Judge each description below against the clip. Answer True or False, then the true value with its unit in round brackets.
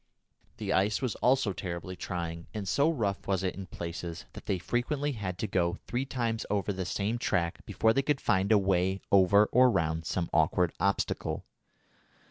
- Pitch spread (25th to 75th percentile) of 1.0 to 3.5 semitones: False (4.2 semitones)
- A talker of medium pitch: False (95 Hz)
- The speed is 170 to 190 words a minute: True (180 wpm)